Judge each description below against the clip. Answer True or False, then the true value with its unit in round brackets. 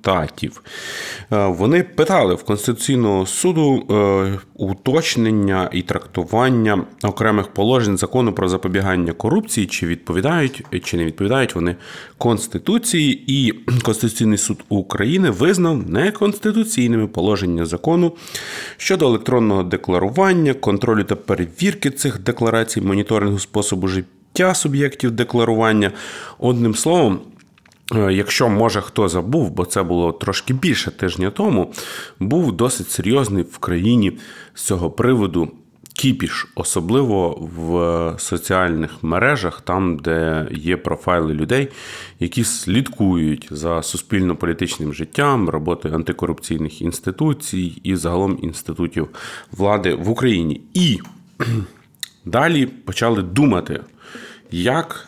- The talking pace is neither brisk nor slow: False (100 wpm)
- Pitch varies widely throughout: True (5.8 semitones)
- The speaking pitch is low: True (100 Hz)